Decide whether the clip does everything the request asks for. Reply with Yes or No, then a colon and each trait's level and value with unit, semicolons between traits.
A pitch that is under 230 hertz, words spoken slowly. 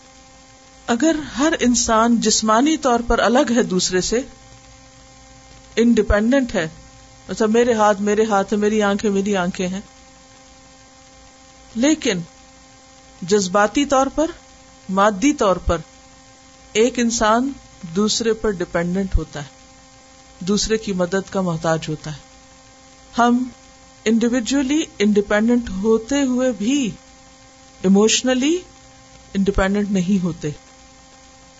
Yes: high, 195 Hz; slow, 100 wpm